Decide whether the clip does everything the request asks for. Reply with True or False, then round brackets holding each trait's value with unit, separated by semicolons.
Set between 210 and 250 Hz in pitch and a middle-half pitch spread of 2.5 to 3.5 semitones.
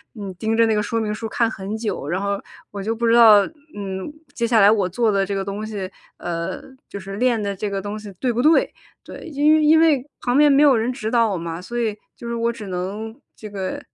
True (220 Hz; 3.1 semitones)